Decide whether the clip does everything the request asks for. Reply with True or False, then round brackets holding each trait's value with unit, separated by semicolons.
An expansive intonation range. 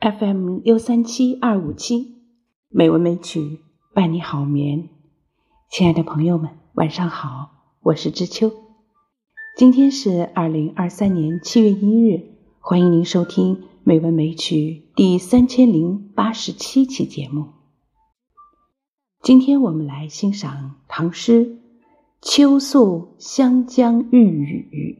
True (7.1 semitones)